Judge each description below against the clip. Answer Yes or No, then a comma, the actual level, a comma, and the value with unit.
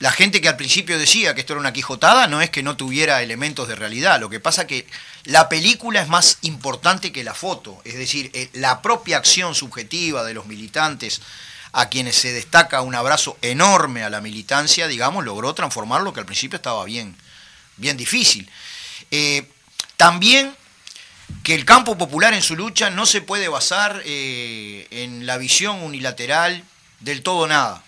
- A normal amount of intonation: No, wide, 5.9 semitones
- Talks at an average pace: Yes, average, 180 wpm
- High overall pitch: No, medium, 145 Hz